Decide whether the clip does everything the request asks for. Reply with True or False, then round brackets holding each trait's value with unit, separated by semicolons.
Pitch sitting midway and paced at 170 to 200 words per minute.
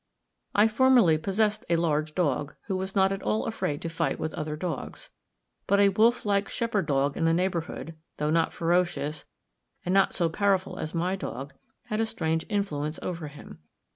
True (175 Hz; 180 wpm)